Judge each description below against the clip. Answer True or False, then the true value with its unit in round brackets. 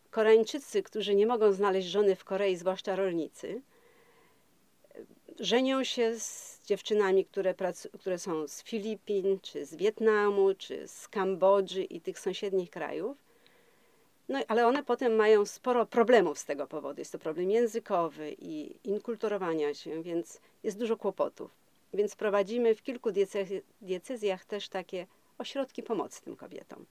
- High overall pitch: True (210 Hz)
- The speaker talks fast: False (140 wpm)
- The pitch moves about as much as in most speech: True (3.8 semitones)